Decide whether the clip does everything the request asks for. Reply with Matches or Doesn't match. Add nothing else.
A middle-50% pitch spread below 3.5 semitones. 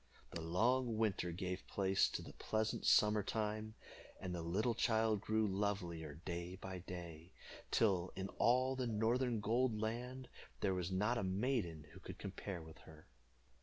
Doesn't match